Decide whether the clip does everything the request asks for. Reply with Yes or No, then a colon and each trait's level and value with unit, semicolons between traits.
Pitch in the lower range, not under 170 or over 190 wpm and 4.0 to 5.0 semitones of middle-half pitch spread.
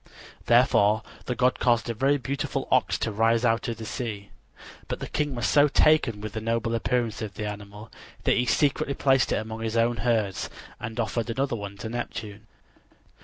No: low, 115 Hz; average, 185 wpm; narrow, 2.4 semitones